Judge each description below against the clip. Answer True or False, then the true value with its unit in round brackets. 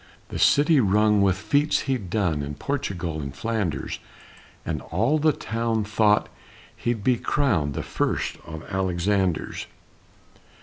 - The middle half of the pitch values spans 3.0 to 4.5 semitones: False (5.0 semitones)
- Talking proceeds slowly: True (130 wpm)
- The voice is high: False (105 Hz)